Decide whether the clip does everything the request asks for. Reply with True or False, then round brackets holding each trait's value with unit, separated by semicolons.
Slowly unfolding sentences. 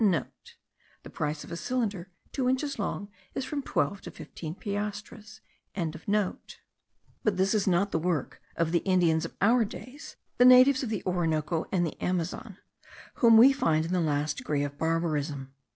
False (165 wpm)